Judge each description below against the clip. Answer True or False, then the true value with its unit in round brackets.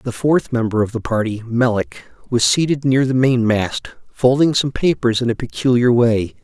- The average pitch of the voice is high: False (125 Hz)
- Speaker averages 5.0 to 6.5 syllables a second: False (4.8 syllables/s)